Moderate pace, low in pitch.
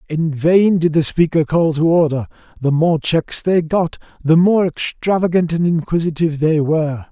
No: average, 170 wpm; medium, 160 Hz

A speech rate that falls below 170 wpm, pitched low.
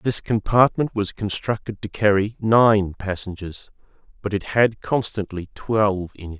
Yes: average, 140 wpm; low, 105 Hz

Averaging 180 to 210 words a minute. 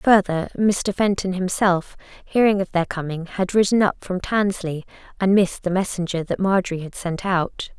No: average, 170 wpm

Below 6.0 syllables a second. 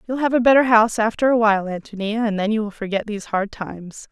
No: 6.1 syllables/s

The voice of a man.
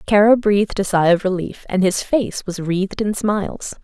No: female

